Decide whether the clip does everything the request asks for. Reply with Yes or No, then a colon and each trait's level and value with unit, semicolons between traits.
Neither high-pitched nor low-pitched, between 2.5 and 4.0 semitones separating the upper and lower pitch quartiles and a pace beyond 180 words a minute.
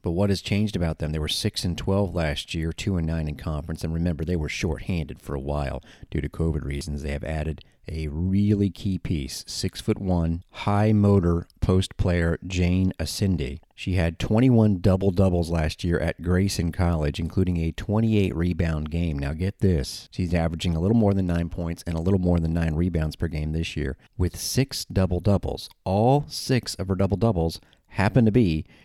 No: very low, 90 Hz; average, 3.3 semitones; average, 195 wpm